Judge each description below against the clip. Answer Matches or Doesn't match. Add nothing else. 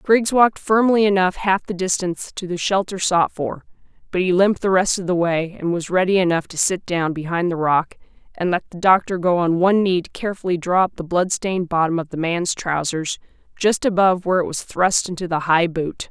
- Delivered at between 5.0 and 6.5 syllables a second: Matches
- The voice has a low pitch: Doesn't match